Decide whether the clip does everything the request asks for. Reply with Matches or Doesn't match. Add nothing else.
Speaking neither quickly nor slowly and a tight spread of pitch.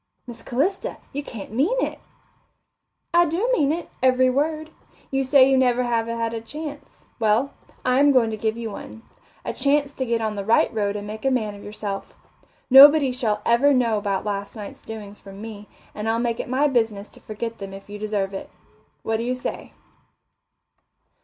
Doesn't match